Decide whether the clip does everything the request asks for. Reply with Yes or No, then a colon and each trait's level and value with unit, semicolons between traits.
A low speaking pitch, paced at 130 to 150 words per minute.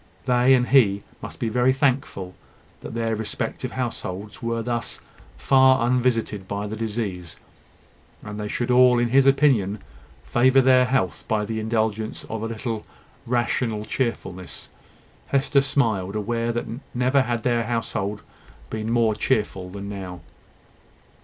Yes: low, 115 Hz; average, 140 wpm